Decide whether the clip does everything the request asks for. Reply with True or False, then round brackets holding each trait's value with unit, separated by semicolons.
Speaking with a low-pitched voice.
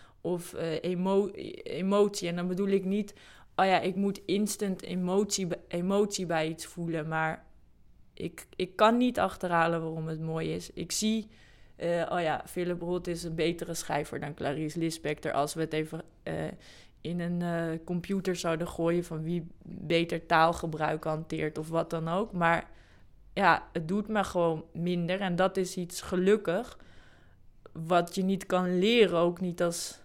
False (170 Hz)